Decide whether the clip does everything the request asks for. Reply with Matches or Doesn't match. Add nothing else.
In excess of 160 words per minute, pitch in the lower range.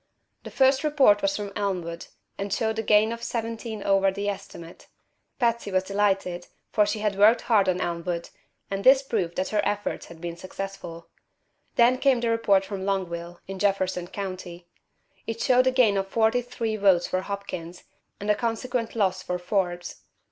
Doesn't match